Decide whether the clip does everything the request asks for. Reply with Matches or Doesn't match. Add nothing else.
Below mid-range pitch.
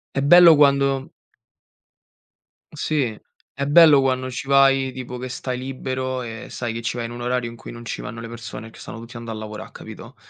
Matches